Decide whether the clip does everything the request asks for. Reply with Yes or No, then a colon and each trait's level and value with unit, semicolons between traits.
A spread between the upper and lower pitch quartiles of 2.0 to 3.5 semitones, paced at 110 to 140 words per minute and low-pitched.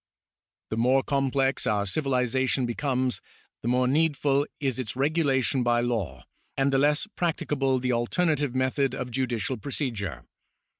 Yes: narrow, 2.5 semitones; slow, 135 wpm; low, 130 Hz